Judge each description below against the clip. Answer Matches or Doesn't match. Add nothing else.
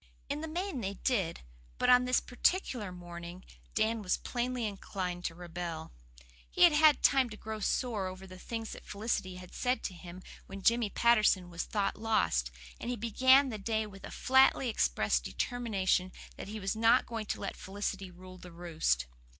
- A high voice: Matches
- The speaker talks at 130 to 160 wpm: Doesn't match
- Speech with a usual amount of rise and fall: Matches